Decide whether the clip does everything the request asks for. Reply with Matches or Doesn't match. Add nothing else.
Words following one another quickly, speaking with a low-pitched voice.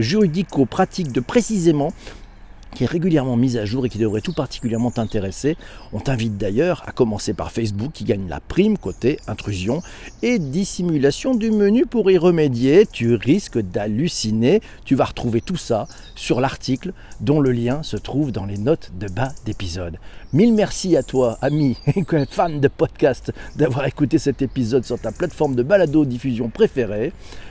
Doesn't match